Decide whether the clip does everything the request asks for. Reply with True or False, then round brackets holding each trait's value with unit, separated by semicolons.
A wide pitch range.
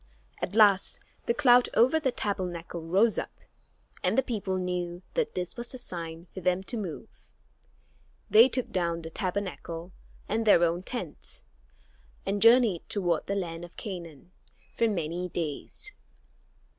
False (4.6 semitones)